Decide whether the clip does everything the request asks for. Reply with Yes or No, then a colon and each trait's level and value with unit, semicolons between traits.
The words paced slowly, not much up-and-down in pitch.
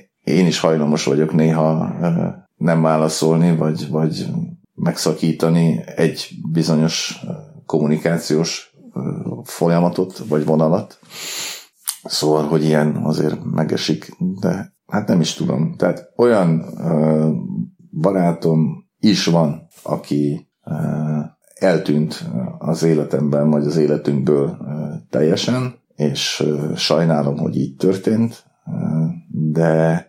Yes: slow, 90 wpm; narrow, 1.9 semitones